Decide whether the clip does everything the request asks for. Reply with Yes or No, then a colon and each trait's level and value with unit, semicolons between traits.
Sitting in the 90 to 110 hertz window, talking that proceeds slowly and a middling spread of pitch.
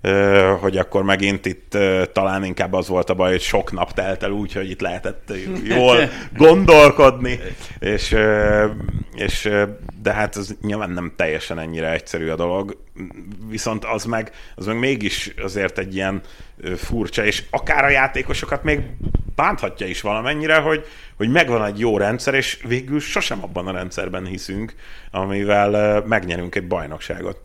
No: low, 100 Hz; average, 150 wpm; average, 3.0 semitones